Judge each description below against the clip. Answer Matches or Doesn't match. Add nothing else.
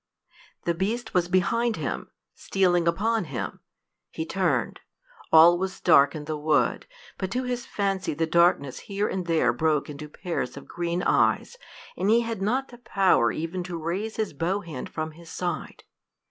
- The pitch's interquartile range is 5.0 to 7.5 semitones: Doesn't match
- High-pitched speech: Doesn't match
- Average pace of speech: Matches